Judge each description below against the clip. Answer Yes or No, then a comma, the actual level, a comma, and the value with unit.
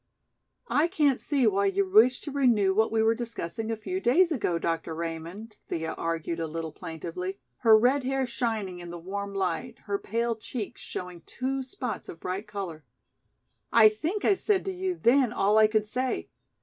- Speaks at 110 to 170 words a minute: No, average, 185 wpm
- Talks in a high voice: Yes, high, 215 Hz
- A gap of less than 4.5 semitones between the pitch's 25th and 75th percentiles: No, wide, 5.6 semitones